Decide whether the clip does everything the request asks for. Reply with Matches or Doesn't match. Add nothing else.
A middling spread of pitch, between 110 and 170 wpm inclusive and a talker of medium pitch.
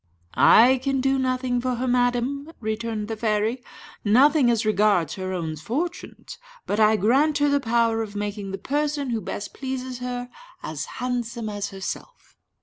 Doesn't match